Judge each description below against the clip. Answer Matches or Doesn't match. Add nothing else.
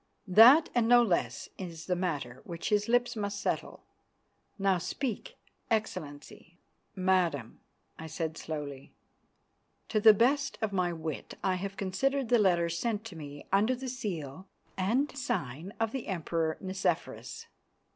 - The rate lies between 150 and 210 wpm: Doesn't match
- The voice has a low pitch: Doesn't match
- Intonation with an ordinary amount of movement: Doesn't match